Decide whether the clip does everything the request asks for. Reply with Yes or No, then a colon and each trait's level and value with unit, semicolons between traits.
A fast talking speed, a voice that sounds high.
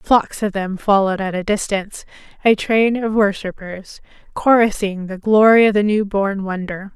No: average, 165 wpm; high, 205 Hz